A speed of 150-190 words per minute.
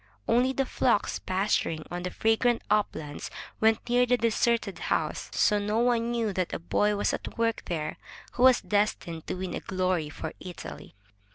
Yes: average, 170 wpm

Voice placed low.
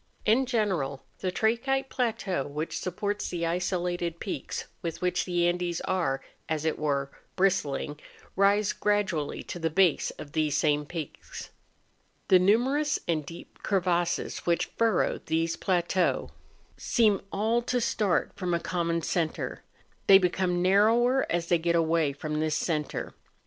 No: medium, 175 Hz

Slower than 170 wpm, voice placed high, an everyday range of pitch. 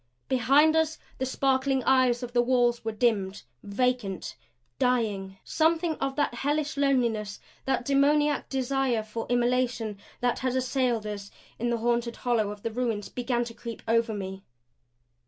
Yes: average, 150 wpm; high, 245 Hz; average, 3.0 semitones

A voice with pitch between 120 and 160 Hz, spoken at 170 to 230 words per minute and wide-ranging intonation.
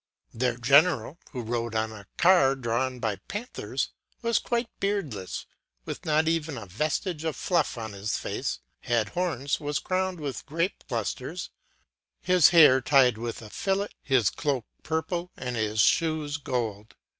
No: medium, 140 Hz; average, 155 wpm; wide, 6.2 semitones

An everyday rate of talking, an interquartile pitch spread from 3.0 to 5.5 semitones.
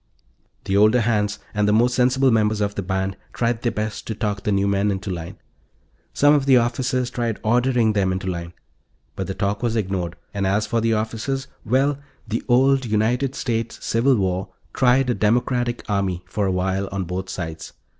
Yes: average, 190 wpm; average, 3.8 semitones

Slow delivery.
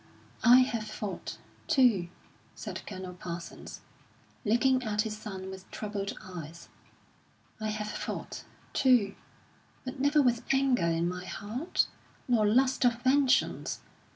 Yes: slow, 125 wpm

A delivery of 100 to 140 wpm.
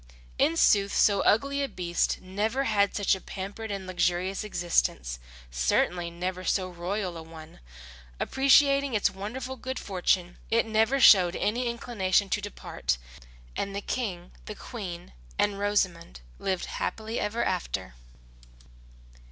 Yes: slow, 135 wpm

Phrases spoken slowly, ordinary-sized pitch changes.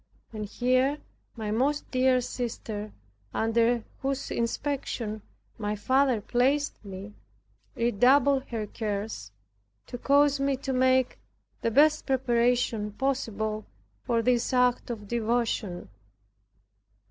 Yes: slow, 105 wpm; average, 3.4 semitones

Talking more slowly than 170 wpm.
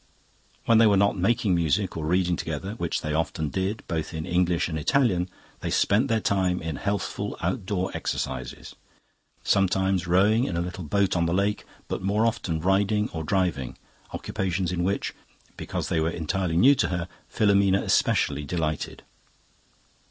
Yes: average, 160 wpm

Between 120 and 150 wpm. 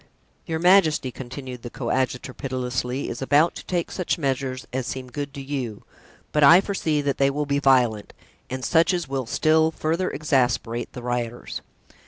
No: average, 170 wpm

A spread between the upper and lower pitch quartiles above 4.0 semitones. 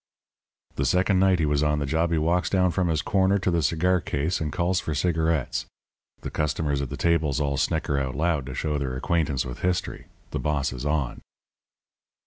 No: average, 3.5 semitones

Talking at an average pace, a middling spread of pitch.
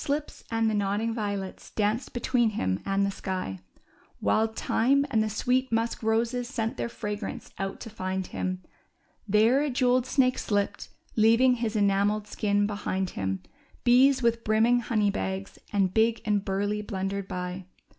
Yes: average, 155 wpm; average, 3.0 semitones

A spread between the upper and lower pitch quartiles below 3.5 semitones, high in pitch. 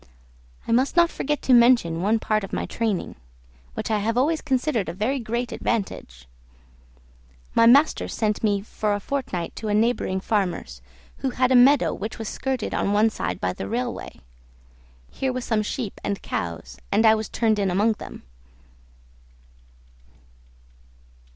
No: average, 4.0 semitones; high, 220 Hz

